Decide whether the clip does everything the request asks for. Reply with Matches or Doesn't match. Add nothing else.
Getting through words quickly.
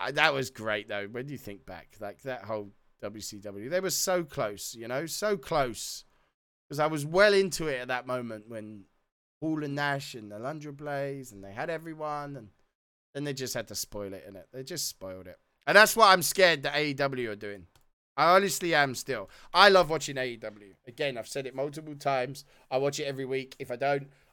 Matches